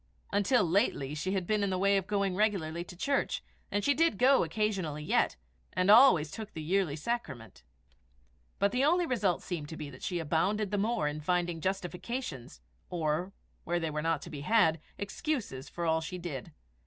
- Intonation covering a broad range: No, average, 4.8 semitones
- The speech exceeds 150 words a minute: Yes, average, 190 wpm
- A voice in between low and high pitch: Yes, medium, 180 Hz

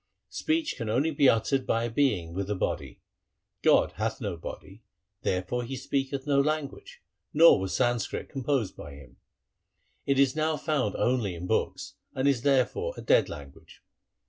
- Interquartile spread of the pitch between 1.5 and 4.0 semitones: No, average, 5.3 semitones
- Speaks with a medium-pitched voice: No, low, 130 Hz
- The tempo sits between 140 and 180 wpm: Yes, average, 170 wpm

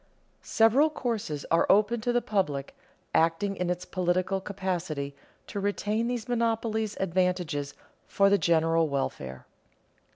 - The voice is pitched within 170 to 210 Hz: Yes, high, 190 Hz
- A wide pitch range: No, average, 4.9 semitones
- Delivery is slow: Yes, slow, 125 wpm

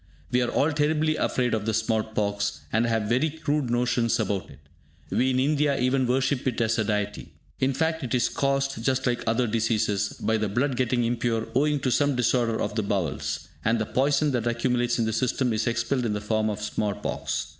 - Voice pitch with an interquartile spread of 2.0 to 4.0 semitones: Yes, average, 3.2 semitones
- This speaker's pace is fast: Yes, fast, 210 wpm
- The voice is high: No, low, 120 Hz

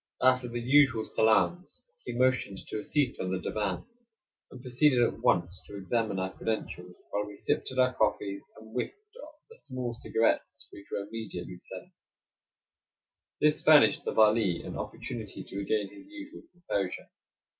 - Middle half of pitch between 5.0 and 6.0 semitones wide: No, average, 4.5 semitones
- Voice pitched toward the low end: Yes, low, 115 Hz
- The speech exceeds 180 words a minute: No, average, 155 wpm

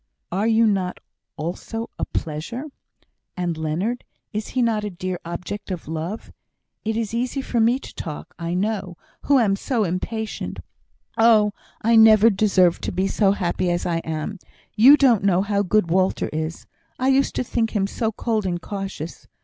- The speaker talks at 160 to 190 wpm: Yes, average, 175 wpm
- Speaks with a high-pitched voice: Yes, high, 200 Hz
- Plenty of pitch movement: No, average, 4.1 semitones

